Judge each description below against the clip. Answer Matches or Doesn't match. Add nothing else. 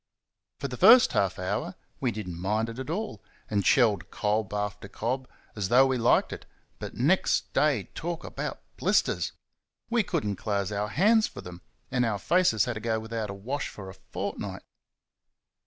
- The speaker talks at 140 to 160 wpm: Doesn't match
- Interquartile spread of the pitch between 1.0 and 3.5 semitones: Doesn't match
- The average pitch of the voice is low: Matches